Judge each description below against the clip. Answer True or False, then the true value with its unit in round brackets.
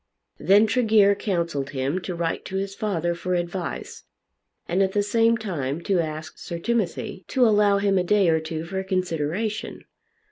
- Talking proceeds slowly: False (170 wpm)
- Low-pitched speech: False (190 Hz)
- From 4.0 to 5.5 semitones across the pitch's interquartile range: False (3.4 semitones)